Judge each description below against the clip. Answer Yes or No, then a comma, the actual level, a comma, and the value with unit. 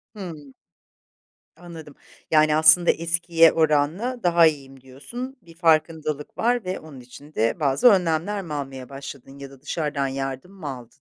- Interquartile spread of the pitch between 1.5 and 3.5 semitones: No, average, 3.9 semitones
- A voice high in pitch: No, medium, 155 Hz